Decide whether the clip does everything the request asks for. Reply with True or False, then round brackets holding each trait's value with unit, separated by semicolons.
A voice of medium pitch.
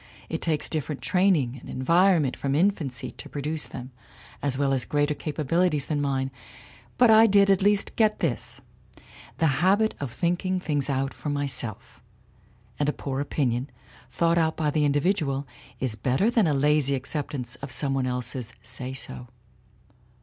True (145 Hz)